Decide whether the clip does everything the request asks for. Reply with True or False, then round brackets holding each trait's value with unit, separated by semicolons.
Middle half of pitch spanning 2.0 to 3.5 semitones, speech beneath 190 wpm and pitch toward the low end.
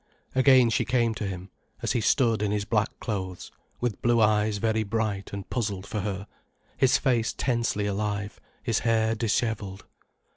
True (2.5 semitones; 160 wpm; 110 Hz)